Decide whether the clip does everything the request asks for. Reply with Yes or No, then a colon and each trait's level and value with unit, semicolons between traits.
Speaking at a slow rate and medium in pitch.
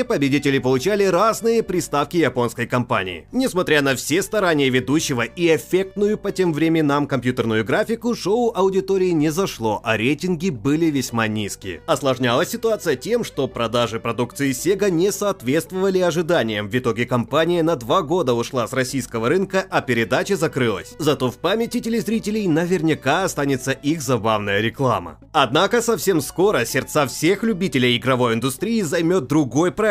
No: average, 140 wpm; medium, 150 Hz